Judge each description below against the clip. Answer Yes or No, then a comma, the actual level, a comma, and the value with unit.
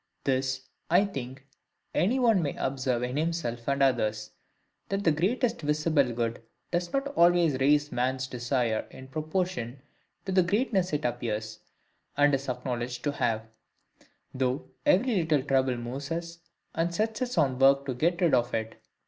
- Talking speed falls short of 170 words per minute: Yes, average, 155 wpm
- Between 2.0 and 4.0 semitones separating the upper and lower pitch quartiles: No, wide, 5.5 semitones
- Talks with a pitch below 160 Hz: Yes, medium, 140 Hz